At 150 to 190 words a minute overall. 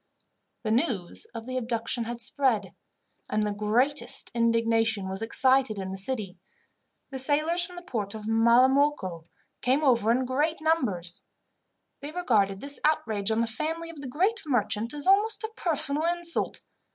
Yes: average, 155 wpm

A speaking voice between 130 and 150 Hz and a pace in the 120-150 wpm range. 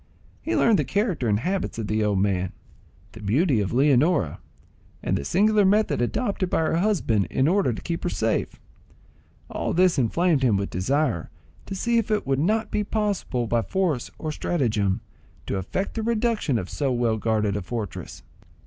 No: medium, 140 Hz; average, 180 wpm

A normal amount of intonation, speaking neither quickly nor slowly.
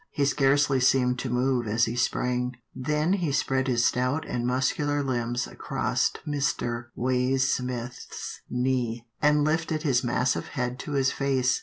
No: narrow, 2.3 semitones; average, 145 wpm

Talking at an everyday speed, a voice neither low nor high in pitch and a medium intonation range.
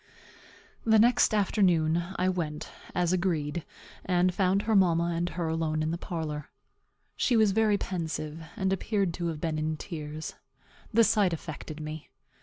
Yes: average, 155 wpm; medium, 175 Hz; average, 3.5 semitones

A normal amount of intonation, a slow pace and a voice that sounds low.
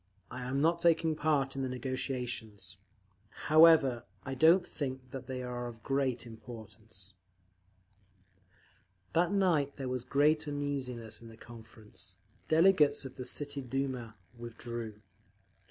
Yes: average, 3.7 semitones; slow, 130 wpm; low, 130 Hz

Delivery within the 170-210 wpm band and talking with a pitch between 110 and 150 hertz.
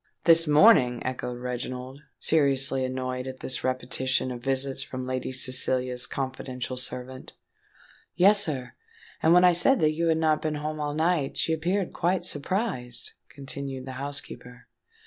No: average, 145 wpm; low, 135 Hz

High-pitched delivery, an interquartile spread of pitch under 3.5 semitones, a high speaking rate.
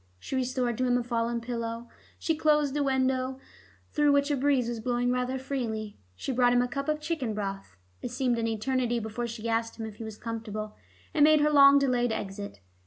Yes: high, 245 Hz; average, 3.0 semitones; fast, 210 wpm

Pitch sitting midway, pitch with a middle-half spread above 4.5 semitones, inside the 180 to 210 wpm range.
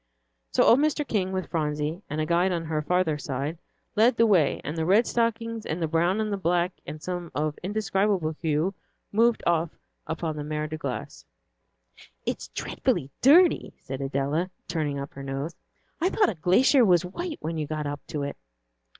Yes: medium, 170 Hz; average, 5.1 semitones; average, 185 wpm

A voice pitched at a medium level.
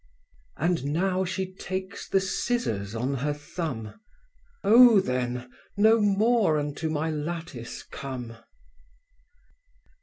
Yes: medium, 160 Hz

